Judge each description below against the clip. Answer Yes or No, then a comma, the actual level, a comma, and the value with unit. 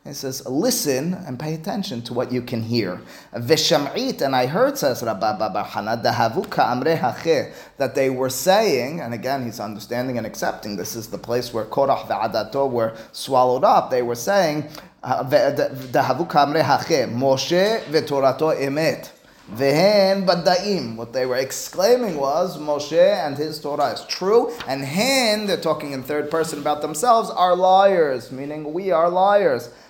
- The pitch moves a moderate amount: No, wide, 6.2 semitones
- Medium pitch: Yes, medium, 145 Hz